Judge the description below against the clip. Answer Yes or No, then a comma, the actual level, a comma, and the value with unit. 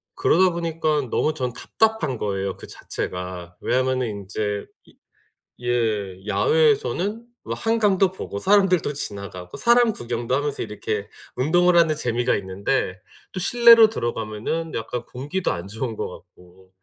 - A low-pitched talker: Yes, low, 130 Hz